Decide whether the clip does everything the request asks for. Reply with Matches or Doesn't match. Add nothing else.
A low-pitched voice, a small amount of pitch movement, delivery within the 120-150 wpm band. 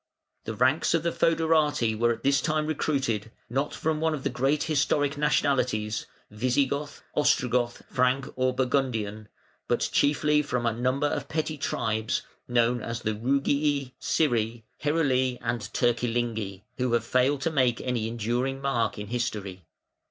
Doesn't match